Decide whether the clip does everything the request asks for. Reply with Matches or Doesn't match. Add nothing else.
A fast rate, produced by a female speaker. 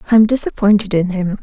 Matches